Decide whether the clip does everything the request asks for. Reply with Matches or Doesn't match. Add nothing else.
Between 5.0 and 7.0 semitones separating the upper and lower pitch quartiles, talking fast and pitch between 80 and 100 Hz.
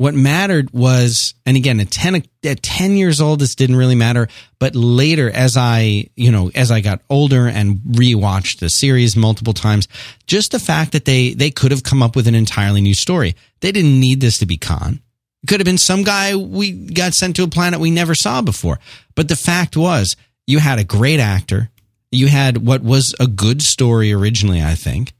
Doesn't match